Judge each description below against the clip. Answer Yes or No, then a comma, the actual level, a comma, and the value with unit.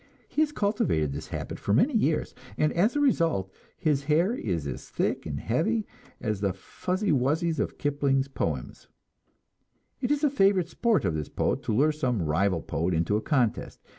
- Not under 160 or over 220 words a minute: Yes, average, 180 wpm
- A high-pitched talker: No, medium, 145 Hz